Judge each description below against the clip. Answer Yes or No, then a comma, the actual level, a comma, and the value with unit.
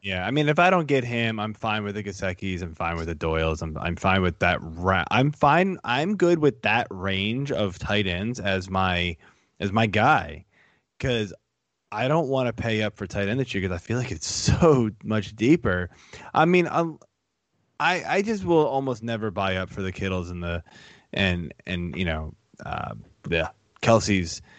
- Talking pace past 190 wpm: Yes, average, 200 wpm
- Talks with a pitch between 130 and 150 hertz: No, low, 100 Hz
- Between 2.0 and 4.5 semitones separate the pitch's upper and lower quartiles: No, wide, 5.6 semitones